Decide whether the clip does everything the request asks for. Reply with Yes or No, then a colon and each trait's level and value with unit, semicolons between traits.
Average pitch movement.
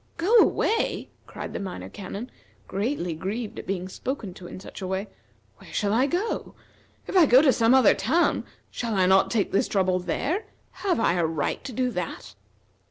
No: wide, 6.2 semitones